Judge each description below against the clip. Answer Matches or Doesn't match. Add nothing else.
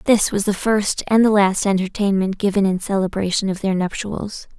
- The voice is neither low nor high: Doesn't match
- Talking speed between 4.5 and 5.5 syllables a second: Matches